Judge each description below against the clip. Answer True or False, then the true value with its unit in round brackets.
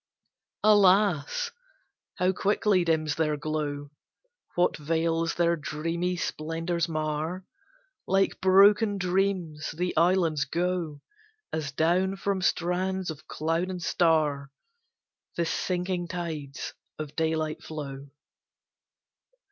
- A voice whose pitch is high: False (170 Hz)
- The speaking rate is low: True (100 wpm)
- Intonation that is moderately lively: True (3.0 semitones)